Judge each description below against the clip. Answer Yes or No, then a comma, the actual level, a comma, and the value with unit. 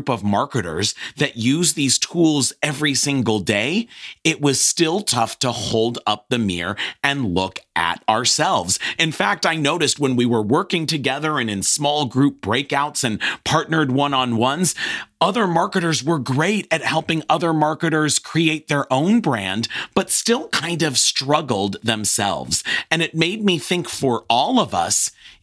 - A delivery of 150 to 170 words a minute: Yes, average, 160 wpm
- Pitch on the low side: No, medium, 145 Hz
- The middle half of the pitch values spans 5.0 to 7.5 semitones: Yes, wide, 5.4 semitones